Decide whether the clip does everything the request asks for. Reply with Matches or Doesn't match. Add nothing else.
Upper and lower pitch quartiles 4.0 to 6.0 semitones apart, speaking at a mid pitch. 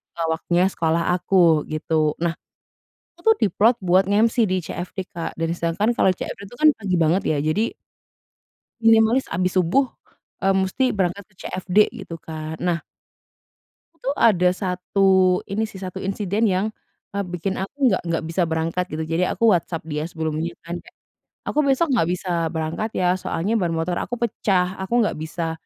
Doesn't match